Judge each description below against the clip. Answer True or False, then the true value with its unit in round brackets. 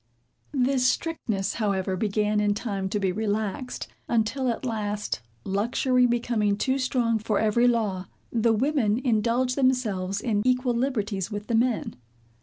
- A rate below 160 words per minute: True (140 wpm)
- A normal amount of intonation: True (3.4 semitones)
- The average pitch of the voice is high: True (225 Hz)